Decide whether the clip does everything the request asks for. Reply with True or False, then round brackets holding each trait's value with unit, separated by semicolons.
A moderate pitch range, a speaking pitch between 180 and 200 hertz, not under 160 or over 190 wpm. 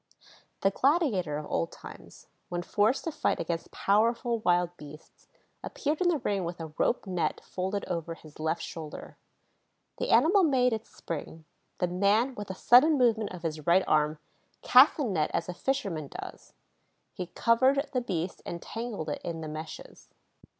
False (6.8 semitones; 190 Hz; 170 wpm)